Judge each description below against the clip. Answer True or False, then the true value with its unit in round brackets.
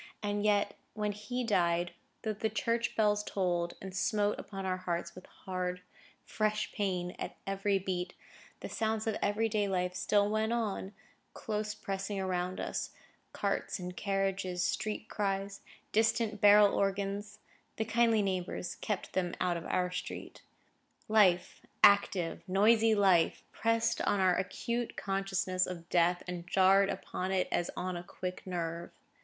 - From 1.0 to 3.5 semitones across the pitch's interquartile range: True (2.5 semitones)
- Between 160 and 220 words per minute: False (145 wpm)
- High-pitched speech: True (195 Hz)